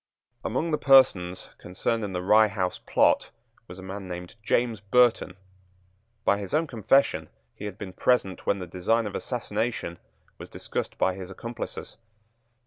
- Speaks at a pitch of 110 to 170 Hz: No, low, 100 Hz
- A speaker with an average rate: Yes, average, 155 wpm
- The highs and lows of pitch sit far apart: No, average, 4.2 semitones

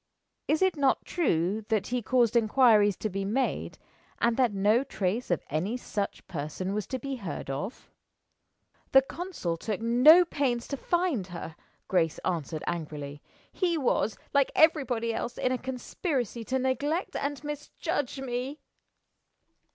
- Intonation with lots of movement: Yes, wide, 5.9 semitones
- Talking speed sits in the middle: Yes, average, 145 wpm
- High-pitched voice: Yes, high, 240 Hz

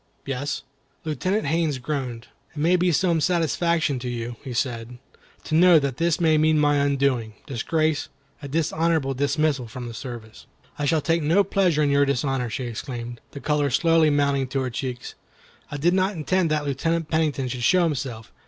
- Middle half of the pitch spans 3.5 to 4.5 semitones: Yes, average, 4.1 semitones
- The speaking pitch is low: No, medium, 145 Hz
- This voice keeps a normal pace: Yes, average, 180 wpm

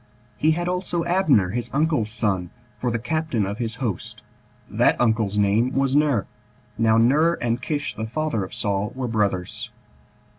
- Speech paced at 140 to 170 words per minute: Yes, average, 160 wpm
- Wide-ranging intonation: Yes, wide, 6.1 semitones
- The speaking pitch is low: Yes, low, 120 Hz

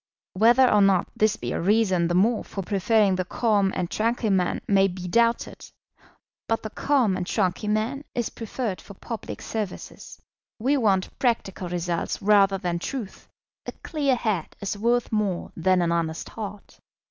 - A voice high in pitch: Yes, high, 205 Hz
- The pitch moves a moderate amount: Yes, average, 3.7 semitones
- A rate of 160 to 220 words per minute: Yes, average, 165 wpm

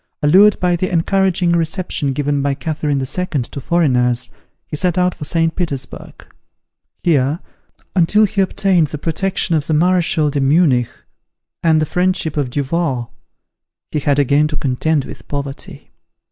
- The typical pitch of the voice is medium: Yes, medium, 155 Hz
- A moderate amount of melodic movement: Yes, average, 4.0 semitones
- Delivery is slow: No, average, 145 wpm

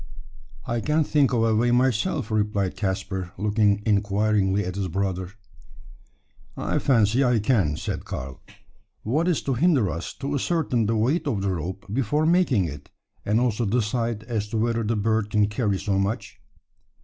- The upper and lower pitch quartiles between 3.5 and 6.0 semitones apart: Yes, average, 3.8 semitones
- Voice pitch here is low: Yes, low, 110 Hz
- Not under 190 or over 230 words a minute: No, average, 165 wpm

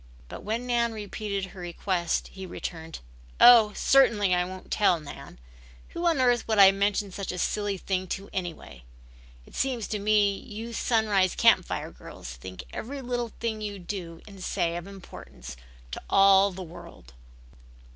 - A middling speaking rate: Yes, average, 165 wpm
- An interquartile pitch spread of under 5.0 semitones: Yes, average, 3.5 semitones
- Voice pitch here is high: Yes, high, 200 Hz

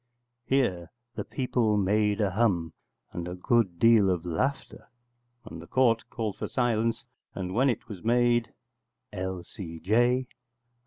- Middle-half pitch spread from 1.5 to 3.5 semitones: No, average, 4.7 semitones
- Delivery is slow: Yes, slow, 130 wpm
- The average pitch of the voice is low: Yes, low, 105 Hz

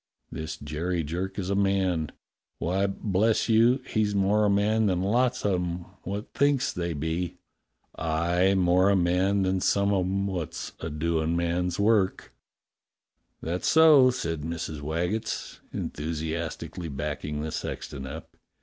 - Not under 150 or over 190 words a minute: No, average, 140 wpm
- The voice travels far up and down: No, average, 3.6 semitones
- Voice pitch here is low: Yes, very low, 90 Hz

